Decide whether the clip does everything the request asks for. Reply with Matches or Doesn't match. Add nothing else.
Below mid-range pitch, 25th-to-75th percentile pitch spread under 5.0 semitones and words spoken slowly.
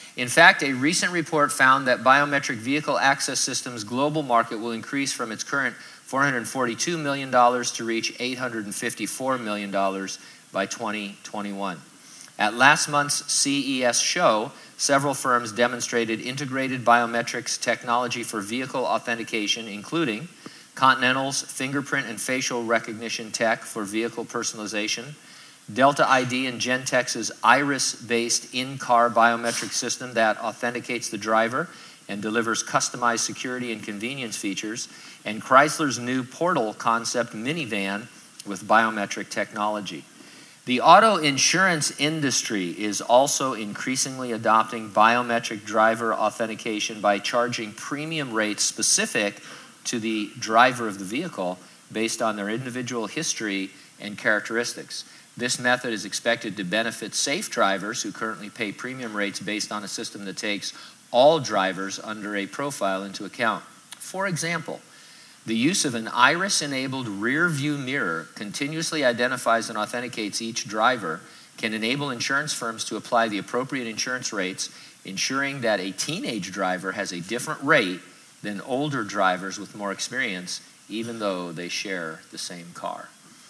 Matches